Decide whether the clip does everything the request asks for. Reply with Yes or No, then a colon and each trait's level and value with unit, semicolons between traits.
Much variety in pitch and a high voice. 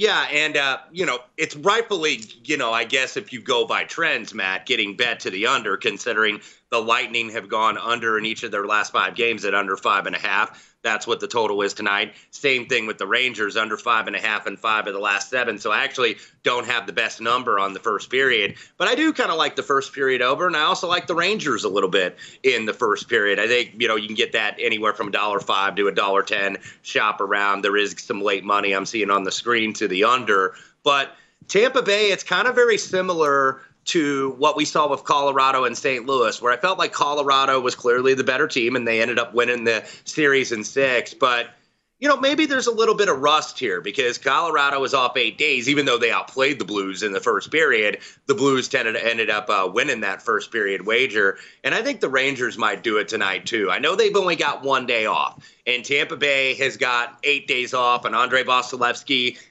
No: wide, 8.1 semitones; low, 135 Hz